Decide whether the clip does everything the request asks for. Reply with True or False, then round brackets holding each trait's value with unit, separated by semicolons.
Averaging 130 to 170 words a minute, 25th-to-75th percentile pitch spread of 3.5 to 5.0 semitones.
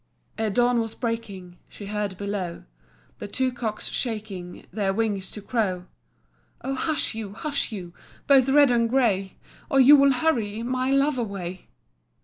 True (150 wpm; 4.4 semitones)